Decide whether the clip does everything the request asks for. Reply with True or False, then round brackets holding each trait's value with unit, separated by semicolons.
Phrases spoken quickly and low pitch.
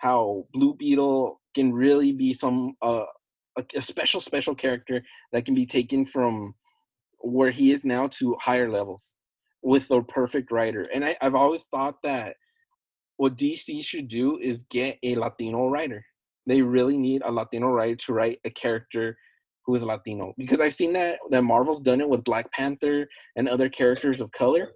False (175 wpm; 130 Hz)